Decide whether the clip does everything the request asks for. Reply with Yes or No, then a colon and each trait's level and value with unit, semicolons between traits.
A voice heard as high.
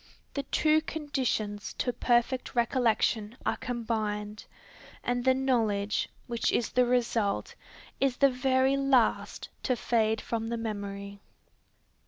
Yes: high, 240 Hz